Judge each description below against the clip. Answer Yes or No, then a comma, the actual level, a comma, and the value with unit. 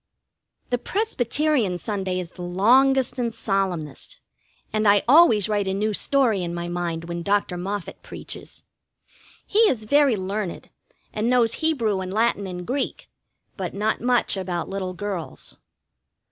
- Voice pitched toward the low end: No, high, 205 Hz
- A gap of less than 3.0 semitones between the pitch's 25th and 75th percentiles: No, average, 4.7 semitones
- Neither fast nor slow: Yes, average, 145 wpm